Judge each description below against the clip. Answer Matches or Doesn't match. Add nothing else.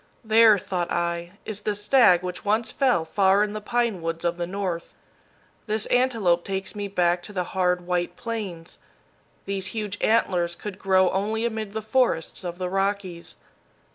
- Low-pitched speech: Doesn't match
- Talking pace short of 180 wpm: Matches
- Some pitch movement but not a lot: Matches